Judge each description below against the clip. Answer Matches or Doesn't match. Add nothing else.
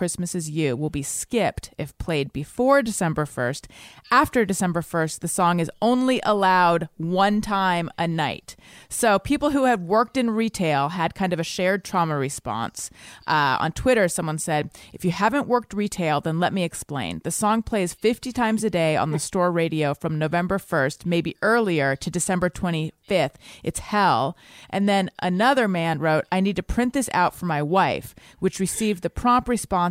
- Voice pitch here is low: Doesn't match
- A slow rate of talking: Doesn't match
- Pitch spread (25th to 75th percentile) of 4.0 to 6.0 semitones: Matches